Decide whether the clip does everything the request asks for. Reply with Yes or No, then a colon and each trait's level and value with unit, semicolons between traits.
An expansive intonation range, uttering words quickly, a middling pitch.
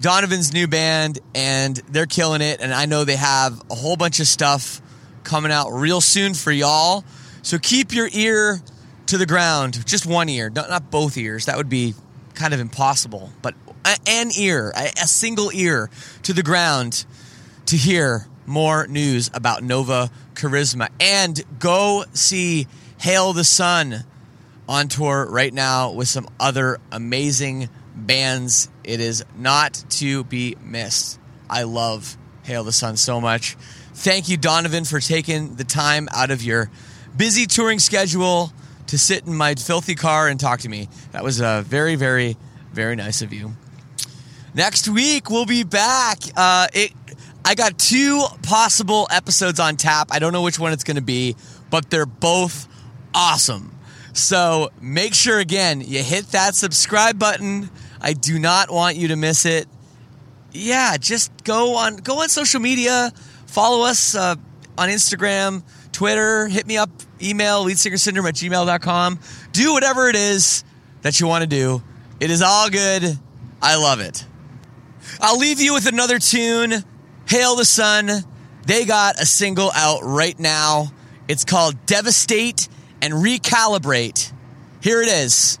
No: wide, 6.7 semitones; average, 155 wpm; medium, 155 Hz